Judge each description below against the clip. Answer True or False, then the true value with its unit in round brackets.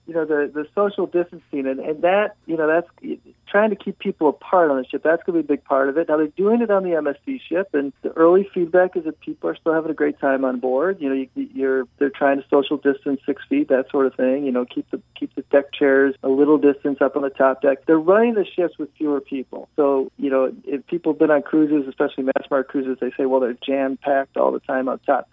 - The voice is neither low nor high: True (145 Hz)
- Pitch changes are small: False (4.2 semitones)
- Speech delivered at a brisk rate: True (270 wpm)